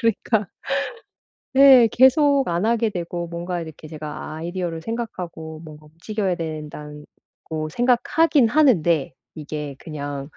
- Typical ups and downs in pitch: No, wide, 6.7 semitones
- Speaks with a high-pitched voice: No, medium, 170 Hz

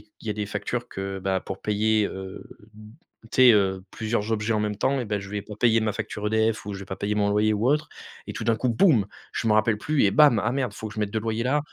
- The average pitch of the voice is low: Yes, low, 110 Hz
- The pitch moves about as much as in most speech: No, narrow, 2.0 semitones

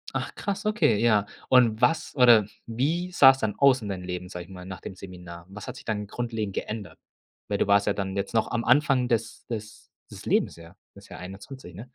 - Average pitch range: Yes, average, 4.5 semitones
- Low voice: Yes, low, 110 Hz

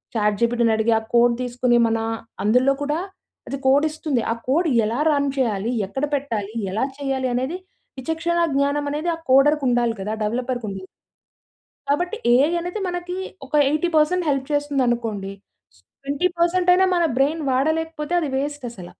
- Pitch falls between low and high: No, very high, 275 Hz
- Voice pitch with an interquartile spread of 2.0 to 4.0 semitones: No, average, 4.5 semitones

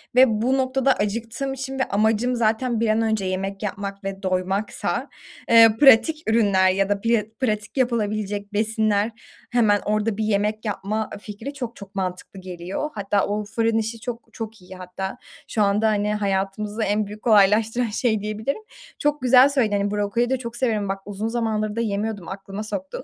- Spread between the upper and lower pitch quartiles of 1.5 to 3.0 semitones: Yes, narrow, 2.5 semitones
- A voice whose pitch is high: Yes, high, 215 Hz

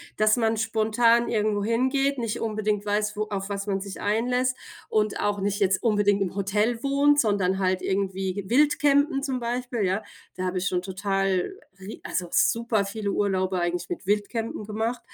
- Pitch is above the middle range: Yes, high, 210 Hz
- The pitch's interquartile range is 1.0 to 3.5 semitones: Yes, average, 3.1 semitones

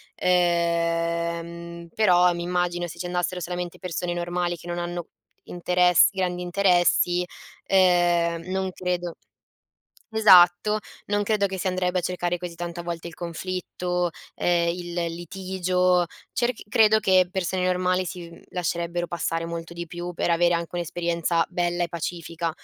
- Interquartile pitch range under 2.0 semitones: Yes, narrow, 1.1 semitones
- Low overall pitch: No, medium, 175 Hz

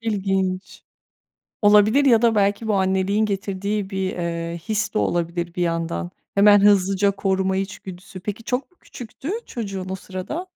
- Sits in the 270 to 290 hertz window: No, high, 195 Hz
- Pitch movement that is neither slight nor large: No, narrow, 2.2 semitones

